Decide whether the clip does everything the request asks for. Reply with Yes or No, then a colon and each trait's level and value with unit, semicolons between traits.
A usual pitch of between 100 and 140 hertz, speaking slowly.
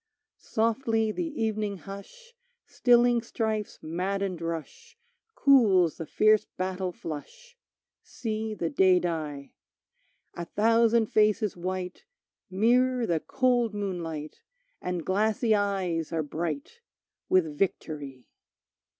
No: high, 200 Hz; slow, 100 wpm